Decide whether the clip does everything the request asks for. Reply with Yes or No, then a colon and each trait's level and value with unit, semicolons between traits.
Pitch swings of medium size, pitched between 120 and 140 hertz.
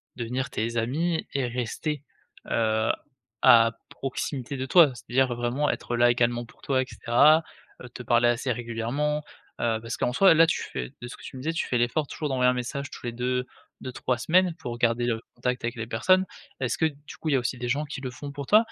Yes: average, 3.2 semitones; low, 125 Hz